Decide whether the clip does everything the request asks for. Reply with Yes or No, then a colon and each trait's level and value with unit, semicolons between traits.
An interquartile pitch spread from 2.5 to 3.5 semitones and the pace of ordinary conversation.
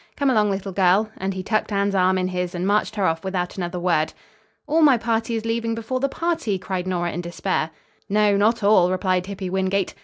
No: average, 3.2 semitones; fast, 215 wpm